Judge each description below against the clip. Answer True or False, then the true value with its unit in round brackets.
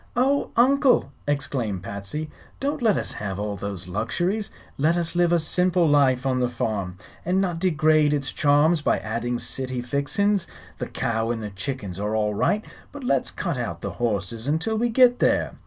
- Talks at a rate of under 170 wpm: False (180 wpm)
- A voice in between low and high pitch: True (145 Hz)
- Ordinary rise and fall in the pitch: False (8.2 semitones)